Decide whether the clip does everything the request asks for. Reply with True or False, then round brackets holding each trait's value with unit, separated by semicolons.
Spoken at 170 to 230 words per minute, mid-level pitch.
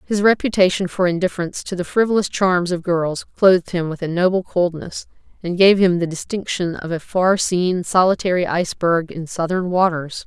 True (175 wpm; 180 Hz)